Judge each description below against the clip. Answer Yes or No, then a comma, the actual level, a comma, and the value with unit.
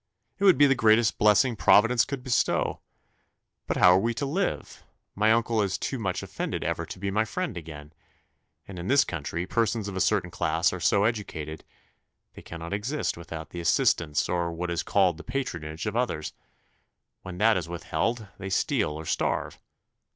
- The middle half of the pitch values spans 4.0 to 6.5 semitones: Yes, average, 5.3 semitones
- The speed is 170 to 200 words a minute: Yes, average, 180 wpm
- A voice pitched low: Yes, low, 100 Hz